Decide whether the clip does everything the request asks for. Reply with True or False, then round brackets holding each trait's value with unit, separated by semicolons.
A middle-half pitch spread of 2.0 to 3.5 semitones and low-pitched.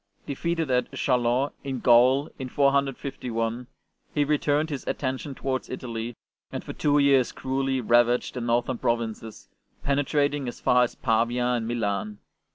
True (2.8 semitones; 125 Hz)